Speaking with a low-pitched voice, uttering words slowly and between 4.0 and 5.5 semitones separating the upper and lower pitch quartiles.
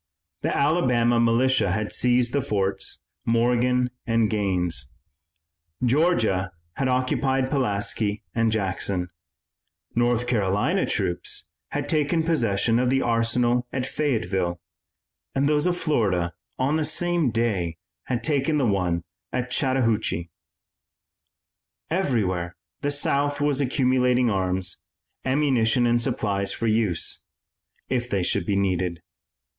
Yes: low, 120 Hz; slow, 115 wpm; average, 5.0 semitones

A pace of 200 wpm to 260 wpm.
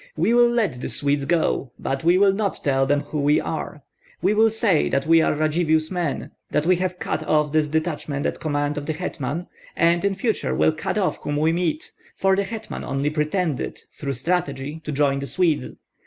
Yes: fast, 205 wpm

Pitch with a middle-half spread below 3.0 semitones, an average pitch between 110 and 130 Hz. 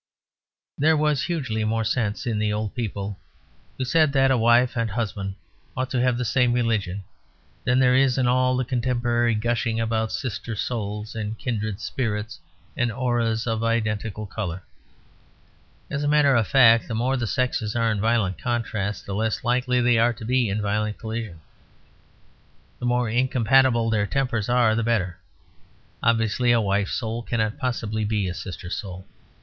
Yes: narrow, 2.6 semitones; low, 115 Hz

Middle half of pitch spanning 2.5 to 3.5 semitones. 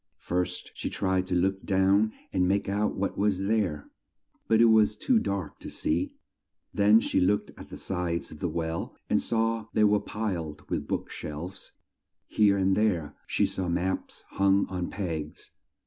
Yes: average, 2.8 semitones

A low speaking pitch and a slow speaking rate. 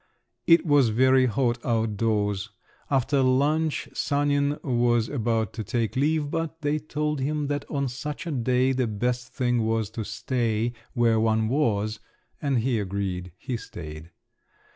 No: low, 125 Hz; average, 155 wpm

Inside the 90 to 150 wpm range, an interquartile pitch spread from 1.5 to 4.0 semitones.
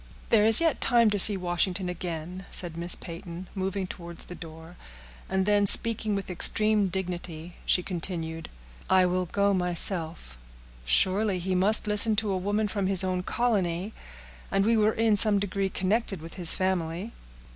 No: average, 160 wpm; average, 2.9 semitones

